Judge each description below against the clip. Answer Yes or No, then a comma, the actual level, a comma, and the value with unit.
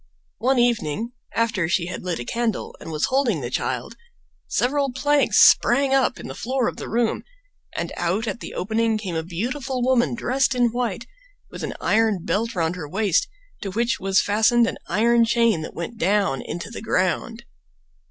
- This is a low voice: No, high, 225 Hz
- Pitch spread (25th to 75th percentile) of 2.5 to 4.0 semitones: No, average, 4.6 semitones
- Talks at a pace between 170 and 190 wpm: Yes, average, 180 wpm